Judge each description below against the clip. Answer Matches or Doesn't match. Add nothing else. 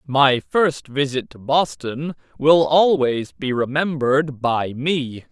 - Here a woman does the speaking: Doesn't match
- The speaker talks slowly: Matches